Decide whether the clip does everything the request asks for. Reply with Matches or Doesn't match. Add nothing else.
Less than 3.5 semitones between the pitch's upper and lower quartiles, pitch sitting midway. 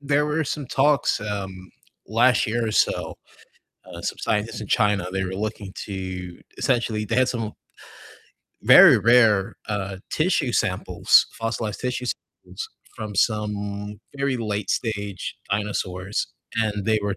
Doesn't match